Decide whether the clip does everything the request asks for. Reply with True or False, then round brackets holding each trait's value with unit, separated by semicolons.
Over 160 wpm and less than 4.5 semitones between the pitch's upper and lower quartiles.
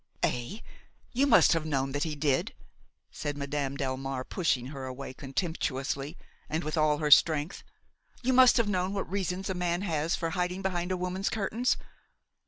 False (170 wpm; 5.0 semitones)